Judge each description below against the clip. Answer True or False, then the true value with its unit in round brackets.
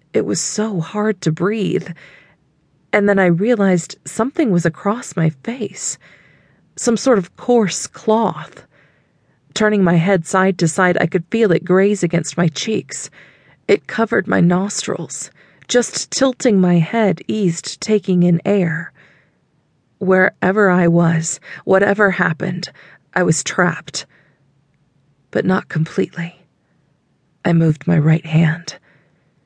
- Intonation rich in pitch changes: False (3.8 semitones)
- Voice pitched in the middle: True (180 Hz)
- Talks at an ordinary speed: False (125 wpm)